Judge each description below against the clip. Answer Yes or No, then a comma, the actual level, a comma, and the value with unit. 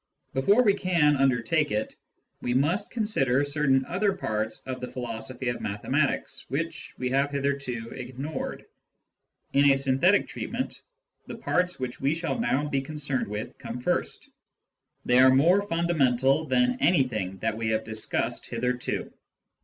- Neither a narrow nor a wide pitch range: Yes, average, 4.2 semitones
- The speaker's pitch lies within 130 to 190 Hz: Yes, low, 135 Hz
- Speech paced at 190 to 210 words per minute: No, average, 145 wpm